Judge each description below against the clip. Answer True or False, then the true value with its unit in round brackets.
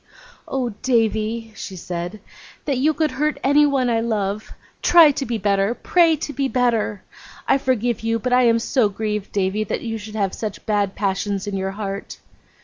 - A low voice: False (225 Hz)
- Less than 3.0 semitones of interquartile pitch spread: False (4.1 semitones)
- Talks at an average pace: True (180 wpm)